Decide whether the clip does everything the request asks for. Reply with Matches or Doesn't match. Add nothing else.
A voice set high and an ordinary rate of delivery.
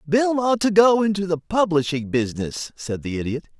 Doesn't match